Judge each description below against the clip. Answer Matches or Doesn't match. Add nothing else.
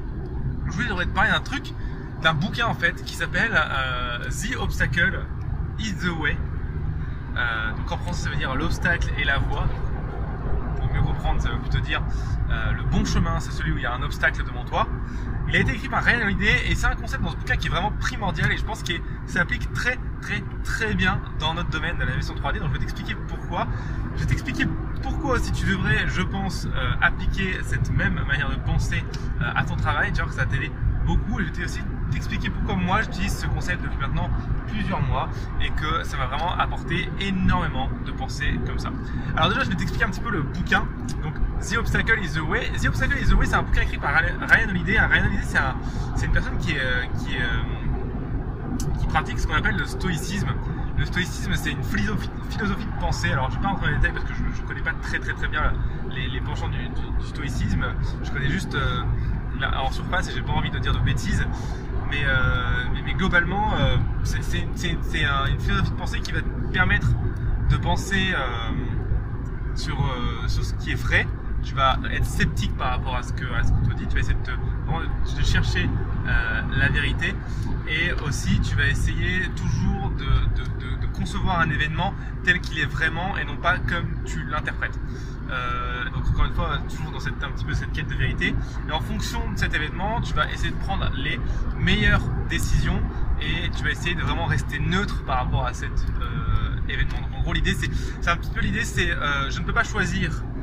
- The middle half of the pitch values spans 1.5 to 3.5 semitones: Matches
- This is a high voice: Doesn't match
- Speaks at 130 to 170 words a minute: Doesn't match